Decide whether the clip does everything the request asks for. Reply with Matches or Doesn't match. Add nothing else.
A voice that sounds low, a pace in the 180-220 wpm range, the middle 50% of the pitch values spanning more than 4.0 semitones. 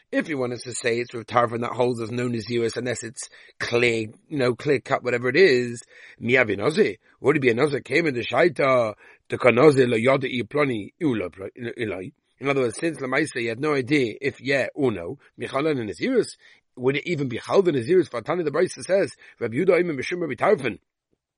Doesn't match